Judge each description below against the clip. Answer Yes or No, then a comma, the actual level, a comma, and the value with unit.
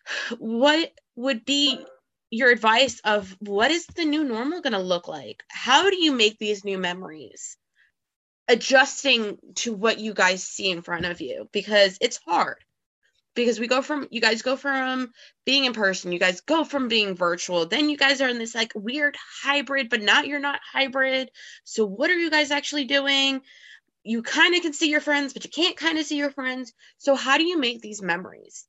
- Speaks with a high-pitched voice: Yes, very high, 260 Hz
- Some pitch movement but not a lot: Yes, average, 5.0 semitones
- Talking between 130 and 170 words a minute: No, average, 200 wpm